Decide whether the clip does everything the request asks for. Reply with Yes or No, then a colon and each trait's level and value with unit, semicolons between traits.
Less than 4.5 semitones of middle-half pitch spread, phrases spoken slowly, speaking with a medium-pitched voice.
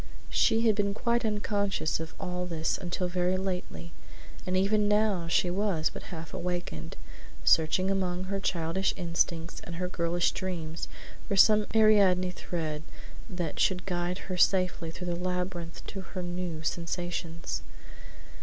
No: narrow, 2.4 semitones; average, 145 wpm; medium, 180 Hz